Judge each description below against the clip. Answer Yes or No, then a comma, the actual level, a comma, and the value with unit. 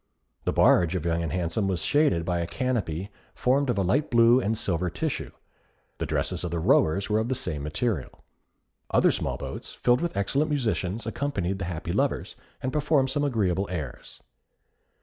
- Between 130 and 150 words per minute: No, average, 180 wpm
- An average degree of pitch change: No, wide, 6.8 semitones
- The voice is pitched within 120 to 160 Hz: No, low, 100 Hz